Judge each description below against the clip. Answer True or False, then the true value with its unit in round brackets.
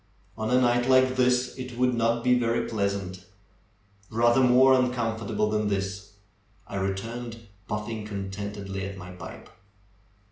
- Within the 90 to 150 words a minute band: True (140 wpm)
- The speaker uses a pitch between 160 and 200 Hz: False (115 Hz)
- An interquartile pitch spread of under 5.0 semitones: True (3.7 semitones)